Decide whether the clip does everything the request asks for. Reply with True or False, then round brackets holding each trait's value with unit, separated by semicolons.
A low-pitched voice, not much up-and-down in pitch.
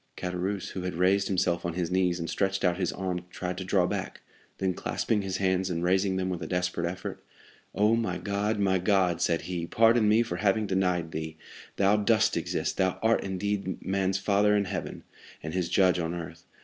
True (95 Hz; 1.9 semitones)